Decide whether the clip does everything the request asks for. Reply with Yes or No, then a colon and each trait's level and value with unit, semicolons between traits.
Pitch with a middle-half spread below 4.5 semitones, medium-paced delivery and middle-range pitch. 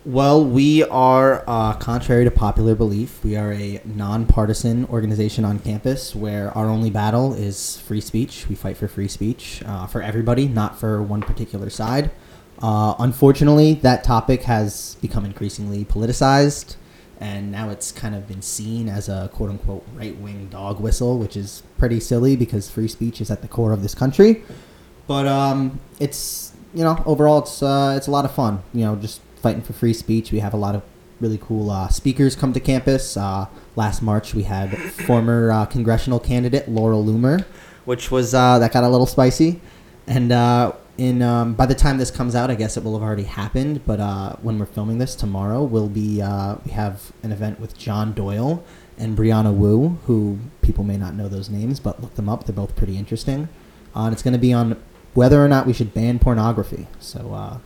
No: average, 3.5 semitones; average, 195 wpm; low, 115 Hz